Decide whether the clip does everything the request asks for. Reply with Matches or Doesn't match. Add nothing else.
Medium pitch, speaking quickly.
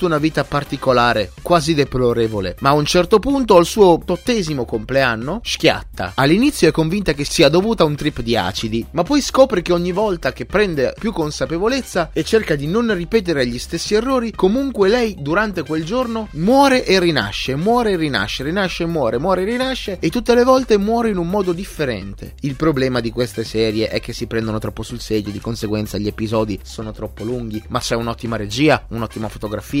Matches